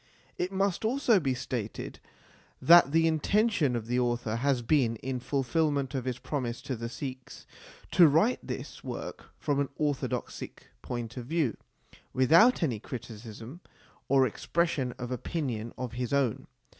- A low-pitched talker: Yes, low, 130 Hz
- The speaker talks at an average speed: Yes, average, 155 wpm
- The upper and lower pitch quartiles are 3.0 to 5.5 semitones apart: Yes, average, 4.8 semitones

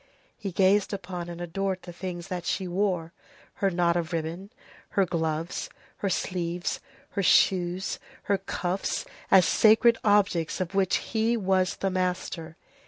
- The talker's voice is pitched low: No, medium, 185 Hz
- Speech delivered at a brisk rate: No, average, 145 wpm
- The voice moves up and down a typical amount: No, narrow, 2.1 semitones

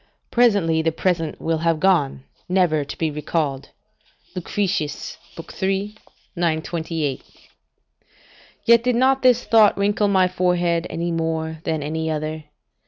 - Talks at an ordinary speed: No, slow, 120 wpm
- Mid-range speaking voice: Yes, medium, 170 Hz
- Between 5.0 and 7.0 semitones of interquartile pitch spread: No, average, 3.6 semitones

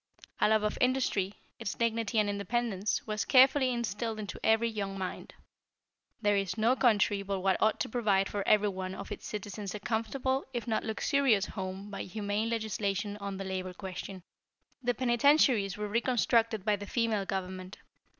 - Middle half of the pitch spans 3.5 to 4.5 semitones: No, average, 2.9 semitones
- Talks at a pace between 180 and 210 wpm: No, average, 165 wpm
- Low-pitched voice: No, high, 210 Hz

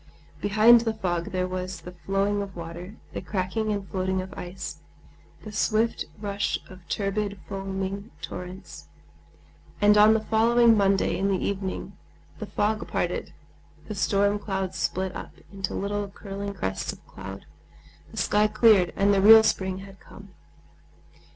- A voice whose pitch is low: No, high, 195 Hz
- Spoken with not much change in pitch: Yes, narrow, 1.9 semitones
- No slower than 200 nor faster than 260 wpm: No, average, 150 wpm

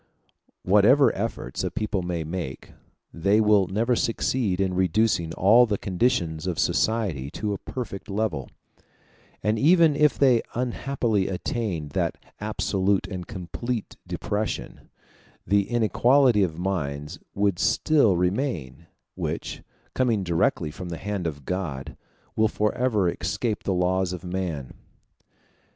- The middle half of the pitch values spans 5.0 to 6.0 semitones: No, average, 4.3 semitones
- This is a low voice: Yes, low, 100 Hz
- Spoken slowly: Yes, slow, 125 wpm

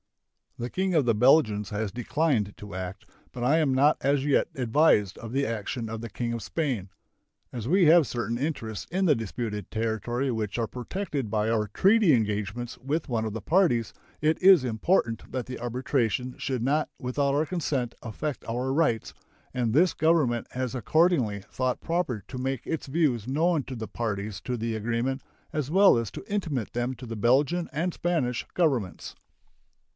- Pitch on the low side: Yes, low, 125 Hz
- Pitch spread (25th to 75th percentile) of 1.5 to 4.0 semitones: No, average, 5.0 semitones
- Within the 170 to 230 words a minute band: Yes, average, 180 wpm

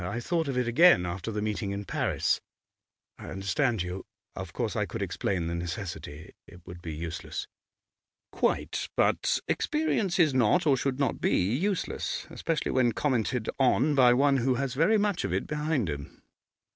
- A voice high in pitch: No, low, 120 Hz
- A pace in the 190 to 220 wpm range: No, average, 170 wpm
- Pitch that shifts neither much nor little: No, wide, 7.9 semitones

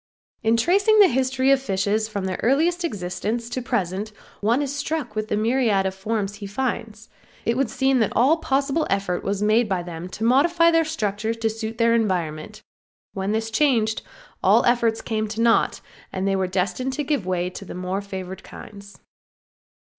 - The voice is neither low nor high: No, high, 220 Hz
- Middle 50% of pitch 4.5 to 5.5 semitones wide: Yes, average, 5.0 semitones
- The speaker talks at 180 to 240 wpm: Yes, average, 185 wpm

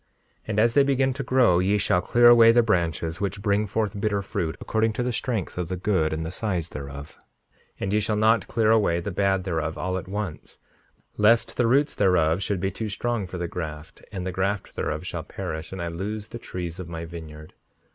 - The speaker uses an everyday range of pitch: Yes, average, 4.4 semitones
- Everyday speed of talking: No, fast, 220 wpm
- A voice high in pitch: No, very low, 95 Hz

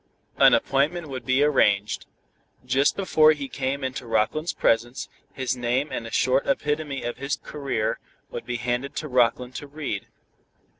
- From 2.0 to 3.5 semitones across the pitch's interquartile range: Yes, average, 3.2 semitones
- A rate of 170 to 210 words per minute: No, average, 155 wpm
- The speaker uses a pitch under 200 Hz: Yes, low, 135 Hz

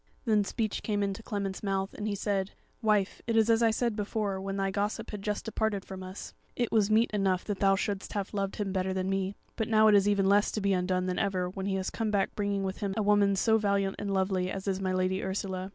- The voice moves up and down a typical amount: No, narrow, 1.6 semitones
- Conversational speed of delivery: No, fast, 255 wpm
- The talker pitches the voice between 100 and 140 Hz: No, high, 200 Hz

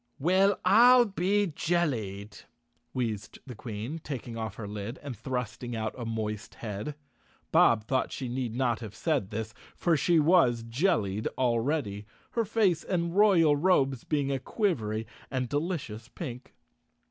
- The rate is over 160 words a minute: No, average, 140 wpm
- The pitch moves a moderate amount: No, wide, 7.2 semitones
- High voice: No, low, 130 Hz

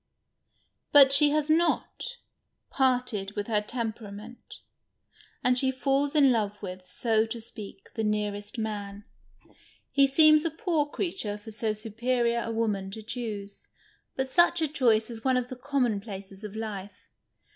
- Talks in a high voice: Yes, high, 230 Hz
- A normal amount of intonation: Yes, average, 4.4 semitones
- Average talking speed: Yes, average, 150 wpm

